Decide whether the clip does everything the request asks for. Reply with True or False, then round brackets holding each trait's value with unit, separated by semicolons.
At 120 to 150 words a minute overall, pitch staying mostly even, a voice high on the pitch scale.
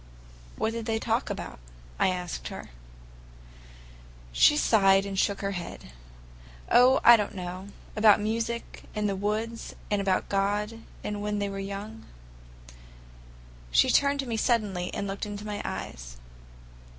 True (145 wpm; 2.3 semitones; 205 Hz)